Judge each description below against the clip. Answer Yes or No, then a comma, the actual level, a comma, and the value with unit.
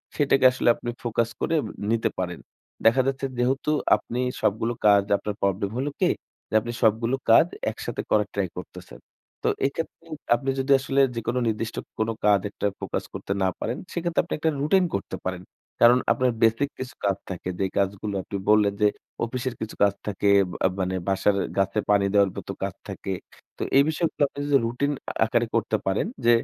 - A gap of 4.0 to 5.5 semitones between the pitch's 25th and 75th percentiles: Yes, average, 4.6 semitones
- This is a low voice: Yes, low, 115 Hz